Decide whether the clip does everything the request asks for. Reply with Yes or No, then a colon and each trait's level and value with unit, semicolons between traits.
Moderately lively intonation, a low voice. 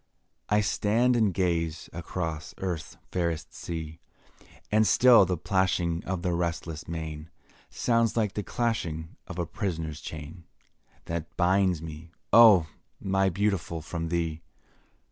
Yes: average, 3.3 semitones; very low, 85 Hz